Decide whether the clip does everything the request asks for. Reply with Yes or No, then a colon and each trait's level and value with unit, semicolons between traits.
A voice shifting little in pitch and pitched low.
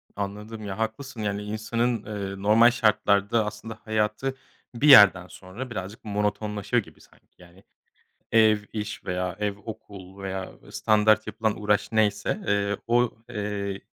Yes: narrow, 1.7 semitones; low, 105 Hz